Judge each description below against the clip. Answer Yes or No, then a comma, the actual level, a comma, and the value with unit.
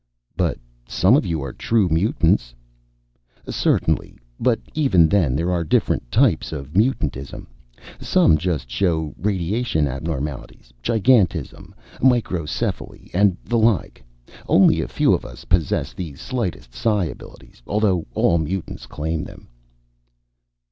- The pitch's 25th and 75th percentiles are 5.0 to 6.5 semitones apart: Yes, wide, 5.5 semitones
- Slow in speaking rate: Yes, slow, 120 wpm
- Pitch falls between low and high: No, very low, 85 Hz